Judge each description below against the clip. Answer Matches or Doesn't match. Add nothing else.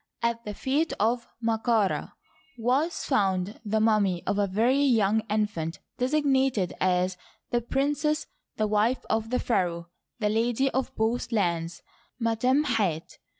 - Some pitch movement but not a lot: Matches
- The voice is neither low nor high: Doesn't match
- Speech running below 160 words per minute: Matches